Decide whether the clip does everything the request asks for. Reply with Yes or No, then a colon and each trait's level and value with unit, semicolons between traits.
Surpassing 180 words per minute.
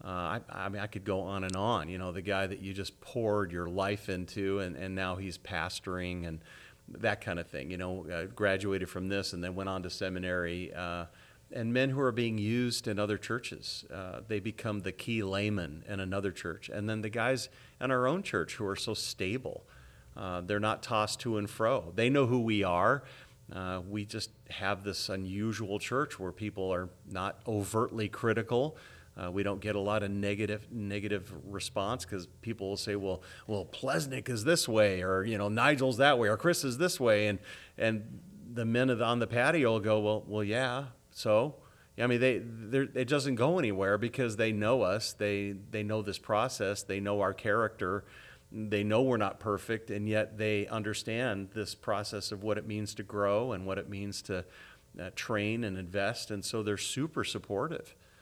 Yes: average, 200 wpm